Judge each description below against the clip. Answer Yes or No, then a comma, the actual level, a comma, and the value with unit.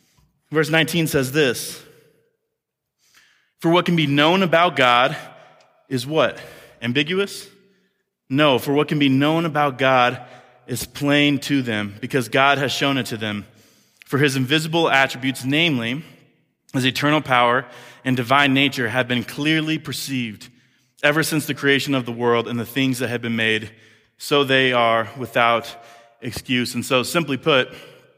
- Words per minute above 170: No, average, 150 wpm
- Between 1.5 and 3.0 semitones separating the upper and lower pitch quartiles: No, average, 3.8 semitones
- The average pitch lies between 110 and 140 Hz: Yes, low, 135 Hz